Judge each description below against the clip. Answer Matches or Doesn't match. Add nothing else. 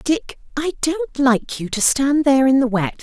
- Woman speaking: Matches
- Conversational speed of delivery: Doesn't match